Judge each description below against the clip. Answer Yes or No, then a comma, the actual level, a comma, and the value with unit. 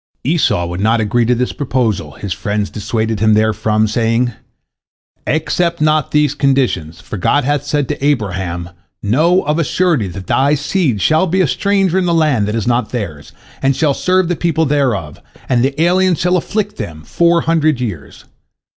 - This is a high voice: No, low, 130 Hz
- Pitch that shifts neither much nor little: No, wide, 7.0 semitones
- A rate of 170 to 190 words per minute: Yes, average, 180 wpm